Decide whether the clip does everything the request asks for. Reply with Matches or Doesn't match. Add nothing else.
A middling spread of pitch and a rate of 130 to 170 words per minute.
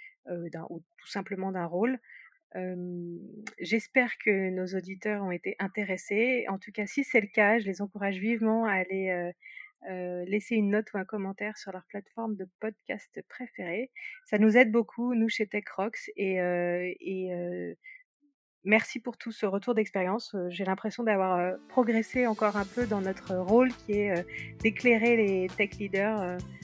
Matches